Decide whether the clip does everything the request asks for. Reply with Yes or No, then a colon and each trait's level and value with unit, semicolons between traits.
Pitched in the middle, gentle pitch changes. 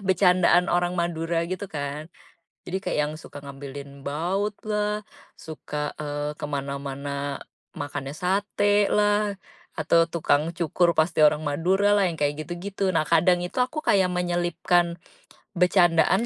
No: medium, 170 Hz; average, 4.2 semitones